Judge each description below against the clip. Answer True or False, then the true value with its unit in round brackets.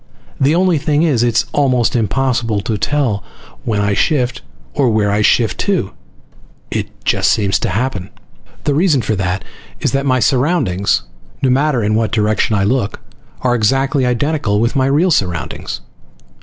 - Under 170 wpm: True (160 wpm)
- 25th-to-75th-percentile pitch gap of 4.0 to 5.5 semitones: True (4.9 semitones)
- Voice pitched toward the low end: True (120 Hz)